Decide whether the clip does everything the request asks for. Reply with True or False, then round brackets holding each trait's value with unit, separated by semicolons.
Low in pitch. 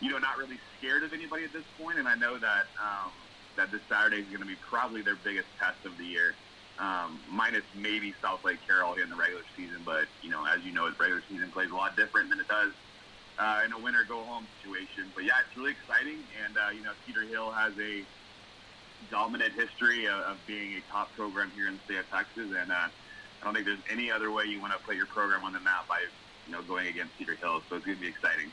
True (110 Hz)